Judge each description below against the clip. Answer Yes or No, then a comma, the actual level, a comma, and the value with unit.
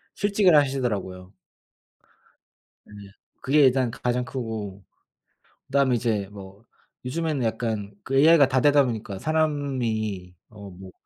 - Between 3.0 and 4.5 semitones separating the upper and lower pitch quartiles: No, wide, 5.4 semitones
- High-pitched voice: No, low, 125 Hz